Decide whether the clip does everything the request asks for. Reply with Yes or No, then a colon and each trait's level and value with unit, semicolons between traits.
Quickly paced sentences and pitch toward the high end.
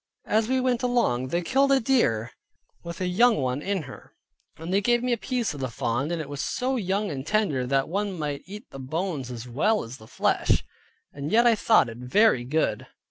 No: fast, 215 wpm; medium, 175 Hz